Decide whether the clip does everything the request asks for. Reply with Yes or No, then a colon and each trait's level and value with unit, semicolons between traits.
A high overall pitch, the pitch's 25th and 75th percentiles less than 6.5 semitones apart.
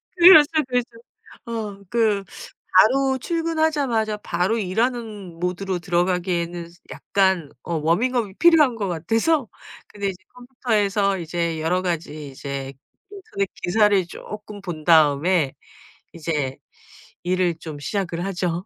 Yes: high, 195 Hz; average, 5.2 semitones